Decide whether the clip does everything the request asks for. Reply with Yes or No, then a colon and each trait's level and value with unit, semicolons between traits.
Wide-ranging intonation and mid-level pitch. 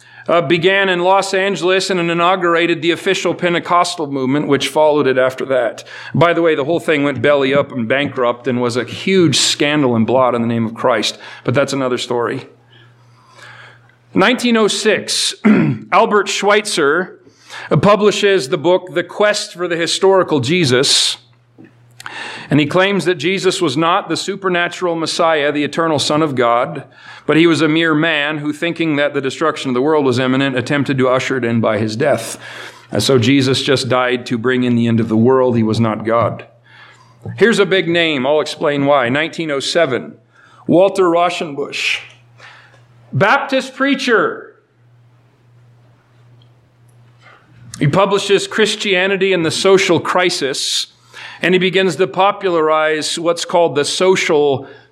Yes: wide, 6.1 semitones; medium, 155 Hz